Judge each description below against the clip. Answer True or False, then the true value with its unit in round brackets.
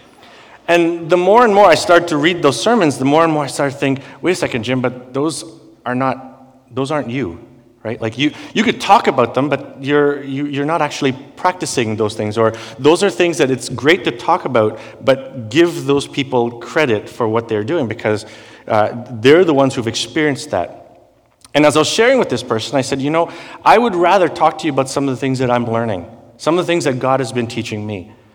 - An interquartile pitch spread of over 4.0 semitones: True (4.5 semitones)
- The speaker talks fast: True (235 wpm)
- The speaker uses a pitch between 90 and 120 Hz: False (135 Hz)